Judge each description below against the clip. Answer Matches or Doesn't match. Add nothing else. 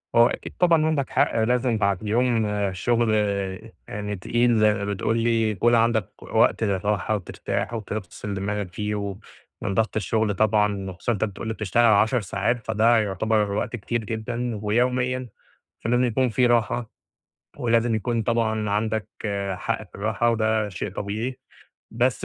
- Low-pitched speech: Matches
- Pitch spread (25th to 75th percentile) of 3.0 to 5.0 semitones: Doesn't match